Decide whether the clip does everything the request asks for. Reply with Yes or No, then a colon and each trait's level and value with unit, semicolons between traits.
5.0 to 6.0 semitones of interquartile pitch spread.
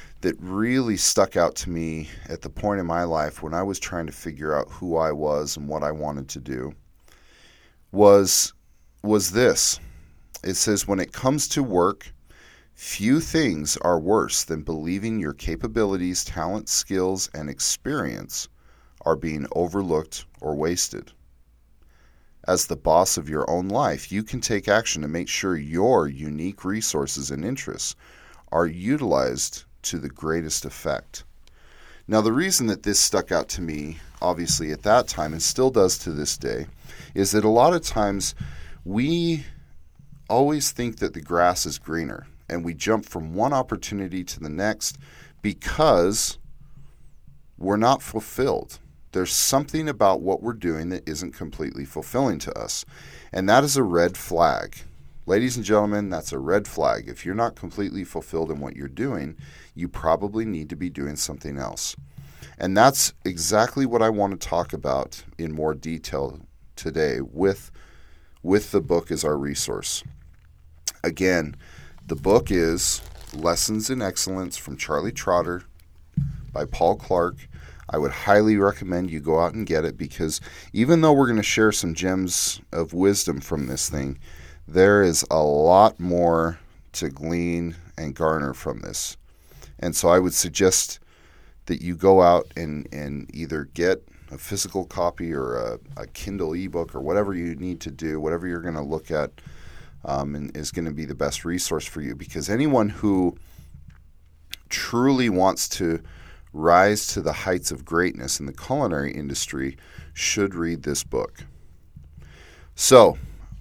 No: average, 4.5 semitones